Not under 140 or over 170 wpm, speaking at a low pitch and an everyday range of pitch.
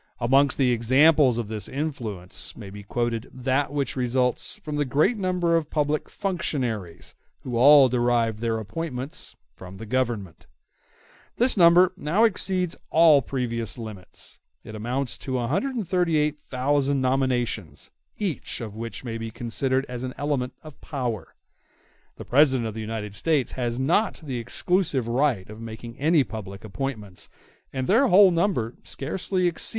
Yes: average, 150 wpm; low, 130 Hz; average, 5.0 semitones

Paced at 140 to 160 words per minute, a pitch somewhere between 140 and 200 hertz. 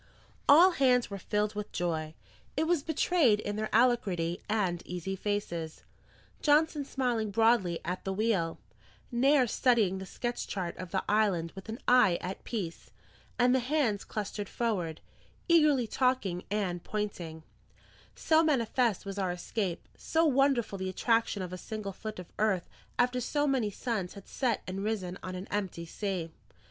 No: average, 155 wpm; high, 210 Hz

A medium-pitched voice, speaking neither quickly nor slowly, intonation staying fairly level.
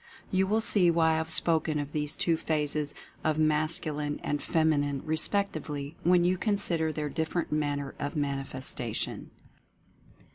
Yes: medium, 155 Hz; average, 145 wpm; narrow, 2.3 semitones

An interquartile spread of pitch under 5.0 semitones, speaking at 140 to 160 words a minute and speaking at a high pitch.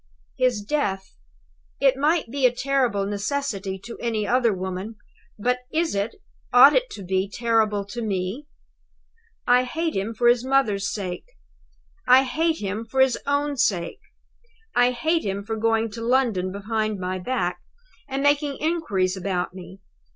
No: average, 5.3 semitones; average, 150 wpm; high, 230 Hz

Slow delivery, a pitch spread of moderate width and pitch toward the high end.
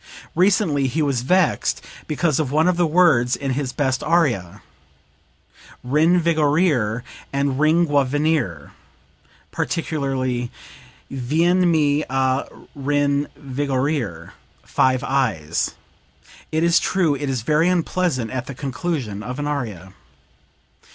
No: slow, 105 wpm; average, 3.8 semitones; medium, 145 Hz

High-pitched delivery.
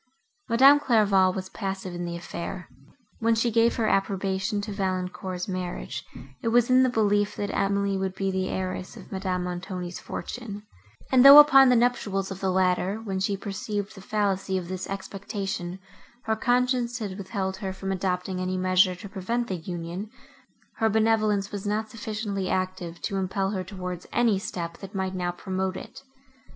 Yes: high, 195 Hz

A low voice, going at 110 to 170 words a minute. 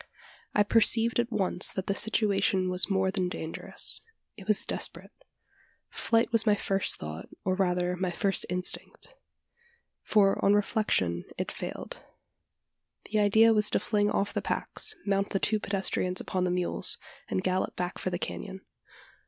No: high, 195 Hz; average, 155 wpm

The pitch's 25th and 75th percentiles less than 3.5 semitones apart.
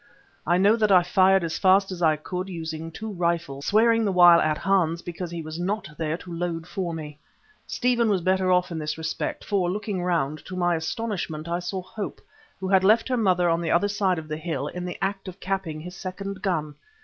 Yes: average, 2.8 semitones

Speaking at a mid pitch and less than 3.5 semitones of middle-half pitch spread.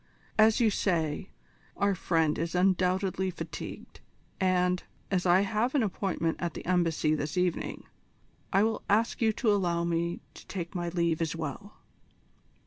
Yes: medium, 180 Hz; average, 2.9 semitones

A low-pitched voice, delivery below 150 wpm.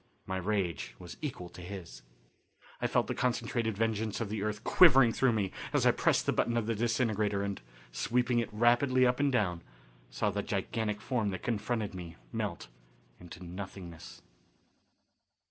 No: low, 105 Hz; average, 165 wpm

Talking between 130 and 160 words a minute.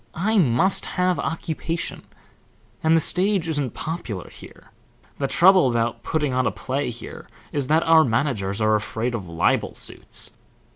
Yes: average, 150 wpm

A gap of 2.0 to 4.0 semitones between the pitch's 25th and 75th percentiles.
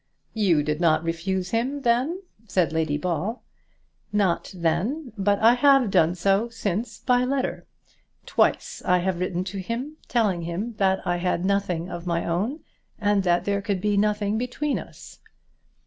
No: average, 5.0 semitones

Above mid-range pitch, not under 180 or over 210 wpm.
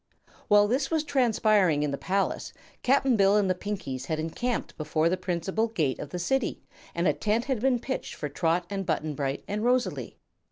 Yes: high, 195 Hz; average, 195 wpm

